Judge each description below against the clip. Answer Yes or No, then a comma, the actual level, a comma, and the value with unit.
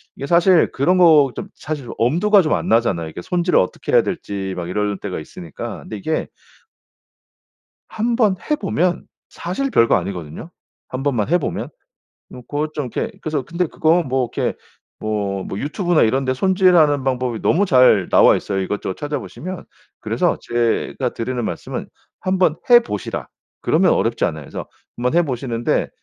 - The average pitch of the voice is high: No, low, 135 Hz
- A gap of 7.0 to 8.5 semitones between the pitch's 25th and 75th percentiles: Yes, wide, 7.8 semitones